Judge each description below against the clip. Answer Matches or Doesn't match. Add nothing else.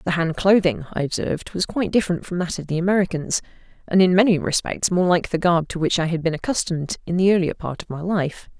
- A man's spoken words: Doesn't match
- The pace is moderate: Doesn't match